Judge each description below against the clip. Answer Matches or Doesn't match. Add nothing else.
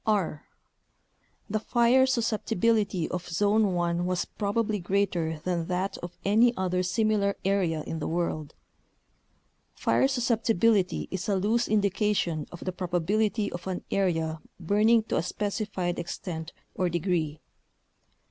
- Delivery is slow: Matches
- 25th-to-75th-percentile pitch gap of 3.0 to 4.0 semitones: Matches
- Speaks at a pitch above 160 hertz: Matches